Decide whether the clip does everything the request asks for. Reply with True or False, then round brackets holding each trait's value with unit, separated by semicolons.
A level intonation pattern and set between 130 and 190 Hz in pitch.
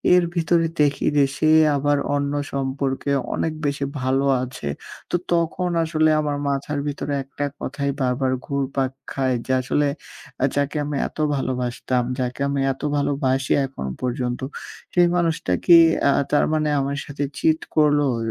True (2.1 semitones; 140 Hz)